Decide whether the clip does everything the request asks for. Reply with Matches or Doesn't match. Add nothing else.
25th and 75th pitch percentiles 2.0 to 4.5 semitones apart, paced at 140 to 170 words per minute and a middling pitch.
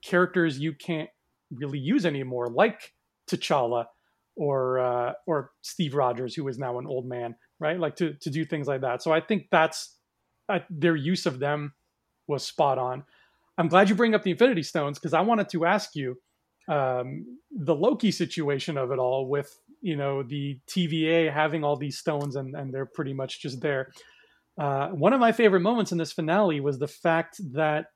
Doesn't match